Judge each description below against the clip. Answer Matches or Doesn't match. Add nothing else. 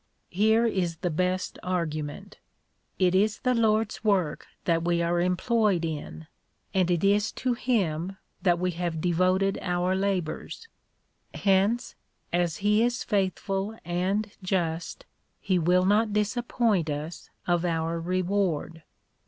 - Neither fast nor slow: Doesn't match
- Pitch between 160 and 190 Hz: Matches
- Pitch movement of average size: Matches